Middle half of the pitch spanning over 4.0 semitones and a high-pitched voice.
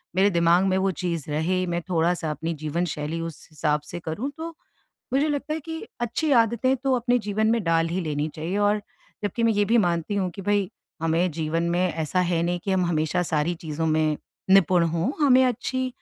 No: average, 4.6 semitones; medium, 180 Hz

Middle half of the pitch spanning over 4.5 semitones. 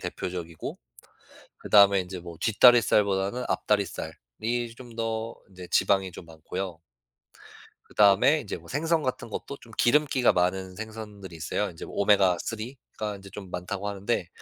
No: average, 3.8 semitones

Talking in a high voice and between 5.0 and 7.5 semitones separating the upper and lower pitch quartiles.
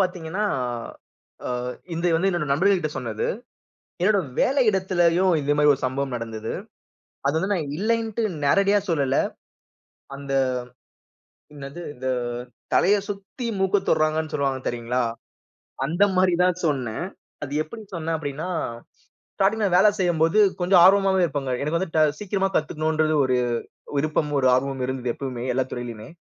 No: medium, 160 Hz; wide, 5.6 semitones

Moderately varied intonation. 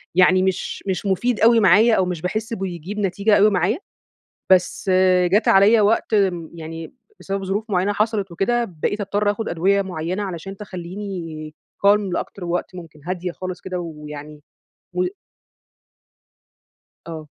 Yes: average, 3.0 semitones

